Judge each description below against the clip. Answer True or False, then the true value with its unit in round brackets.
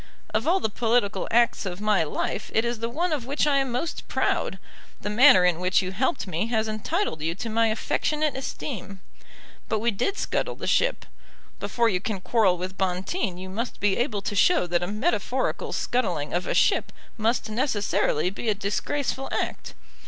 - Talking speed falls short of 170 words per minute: False (190 wpm)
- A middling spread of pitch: True (4.7 semitones)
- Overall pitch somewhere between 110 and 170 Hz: False (220 Hz)